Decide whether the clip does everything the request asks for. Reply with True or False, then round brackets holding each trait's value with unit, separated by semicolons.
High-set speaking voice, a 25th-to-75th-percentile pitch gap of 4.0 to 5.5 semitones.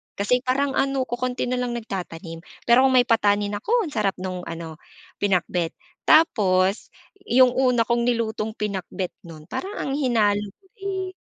True (230 Hz; 4.7 semitones)